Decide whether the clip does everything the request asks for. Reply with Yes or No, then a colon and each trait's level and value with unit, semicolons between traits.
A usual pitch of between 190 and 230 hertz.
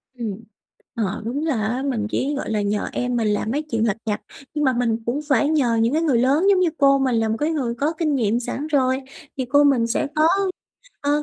No: very high, 255 Hz